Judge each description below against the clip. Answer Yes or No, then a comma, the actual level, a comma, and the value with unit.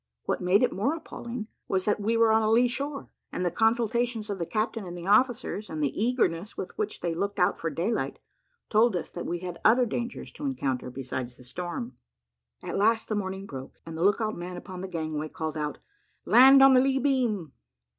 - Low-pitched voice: No, high, 205 Hz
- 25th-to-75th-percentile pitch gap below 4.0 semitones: No, wide, 5.4 semitones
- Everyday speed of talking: No, fast, 210 wpm